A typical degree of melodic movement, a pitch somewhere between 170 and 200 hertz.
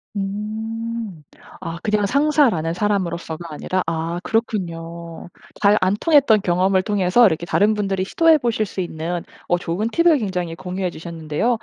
Yes: average, 4.3 semitones; high, 190 Hz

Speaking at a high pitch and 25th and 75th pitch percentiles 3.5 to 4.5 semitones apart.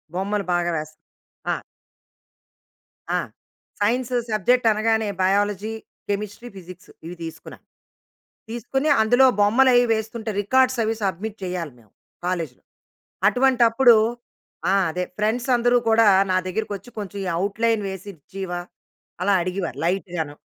Yes: high, 205 Hz; average, 3.8 semitones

